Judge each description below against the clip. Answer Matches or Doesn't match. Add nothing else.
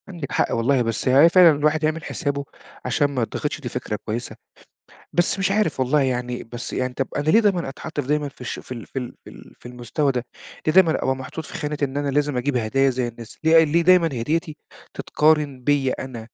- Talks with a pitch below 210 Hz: Matches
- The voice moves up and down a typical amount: Matches